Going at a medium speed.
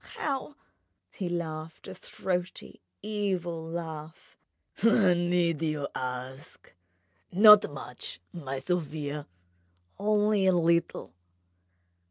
No: slow, 85 wpm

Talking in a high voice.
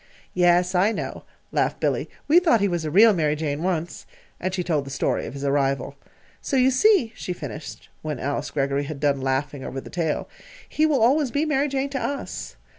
No: medium, 175 Hz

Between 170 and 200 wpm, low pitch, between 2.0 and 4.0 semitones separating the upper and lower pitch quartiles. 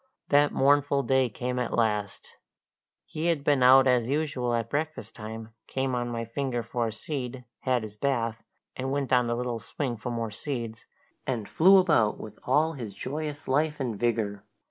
Yes: average, 180 wpm; low, 125 Hz; average, 3.6 semitones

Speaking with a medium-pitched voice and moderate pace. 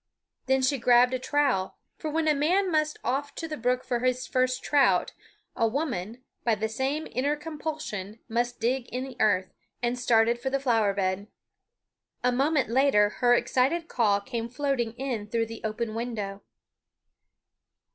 No: very high, 250 Hz; average, 165 wpm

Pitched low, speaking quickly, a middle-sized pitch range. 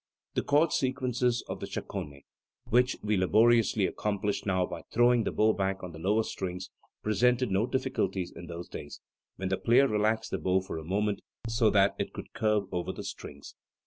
No: low, 105 Hz; average, 185 wpm; average, 4.1 semitones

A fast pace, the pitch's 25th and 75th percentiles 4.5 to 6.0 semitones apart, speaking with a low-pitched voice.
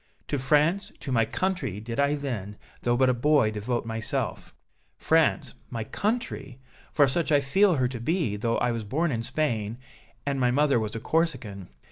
No: average, 180 wpm; average, 4.8 semitones; low, 130 Hz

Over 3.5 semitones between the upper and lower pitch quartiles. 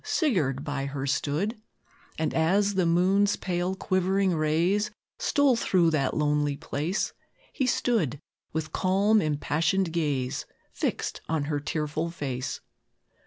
Yes: average, 4.7 semitones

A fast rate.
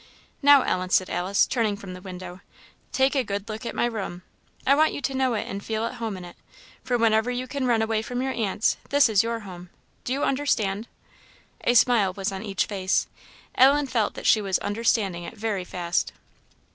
Yes: fast, 210 wpm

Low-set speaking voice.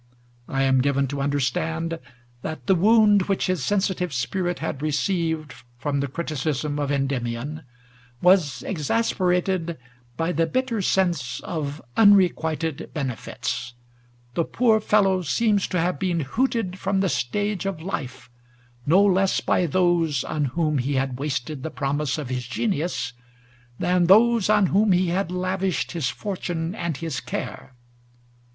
No: medium, 165 Hz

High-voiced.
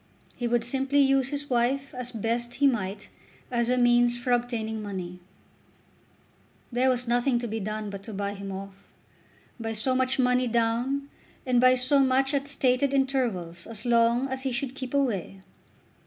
Yes: high, 245 Hz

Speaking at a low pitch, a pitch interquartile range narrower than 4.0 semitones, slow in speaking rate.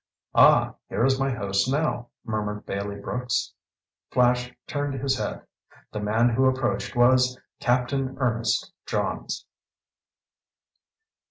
Yes: low, 125 Hz; average, 2.9 semitones; slow, 110 wpm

